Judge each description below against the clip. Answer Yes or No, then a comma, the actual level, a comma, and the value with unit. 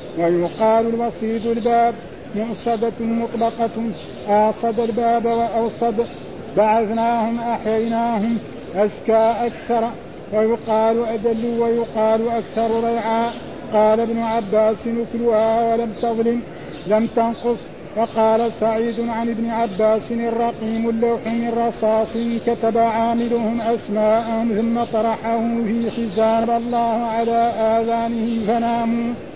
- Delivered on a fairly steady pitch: Yes, narrow, 0.9 semitones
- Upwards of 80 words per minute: Yes, average, 90 wpm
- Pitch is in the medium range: No, high, 230 Hz